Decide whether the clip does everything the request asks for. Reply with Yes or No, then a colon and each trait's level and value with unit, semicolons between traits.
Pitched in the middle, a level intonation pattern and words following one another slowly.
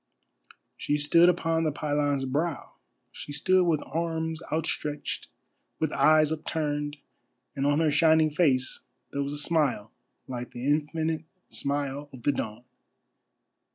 Yes: medium, 150 Hz; narrow, 2.2 semitones; slow, 130 wpm